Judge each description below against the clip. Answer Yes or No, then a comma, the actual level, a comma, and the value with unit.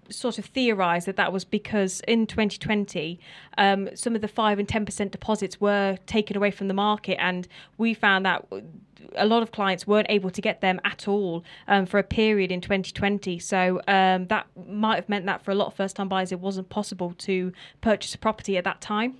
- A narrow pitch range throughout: Yes, narrow, 2.2 semitones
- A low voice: No, high, 200 Hz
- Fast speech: Yes, fast, 215 wpm